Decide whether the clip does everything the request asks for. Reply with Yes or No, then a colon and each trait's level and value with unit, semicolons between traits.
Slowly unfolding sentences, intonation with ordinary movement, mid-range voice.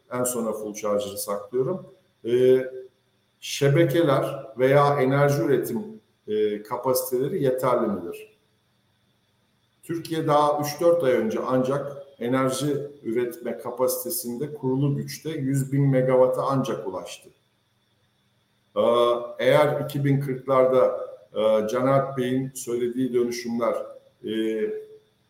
No: slow, 90 wpm; average, 3.1 semitones; low, 130 Hz